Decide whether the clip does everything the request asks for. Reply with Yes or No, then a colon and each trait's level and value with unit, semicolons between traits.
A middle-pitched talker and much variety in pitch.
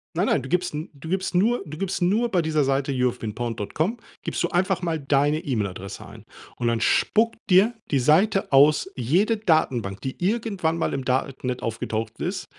Yes: medium, 155 Hz; wide, 6.6 semitones